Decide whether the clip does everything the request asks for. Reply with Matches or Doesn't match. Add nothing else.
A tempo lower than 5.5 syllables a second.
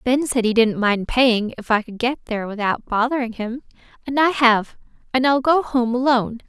Matches